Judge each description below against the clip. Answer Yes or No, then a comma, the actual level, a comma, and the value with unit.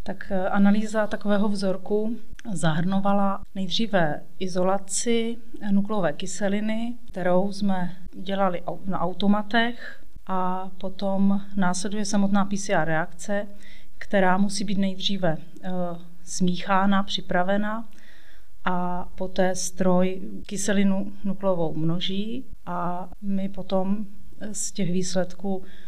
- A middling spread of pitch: No, narrow, 1.8 semitones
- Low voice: No, high, 195 Hz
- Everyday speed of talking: No, slow, 90 wpm